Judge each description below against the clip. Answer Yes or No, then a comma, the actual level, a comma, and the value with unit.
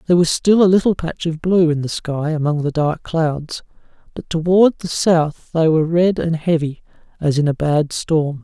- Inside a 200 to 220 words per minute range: Yes, fast, 205 wpm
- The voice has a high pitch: No, medium, 160 Hz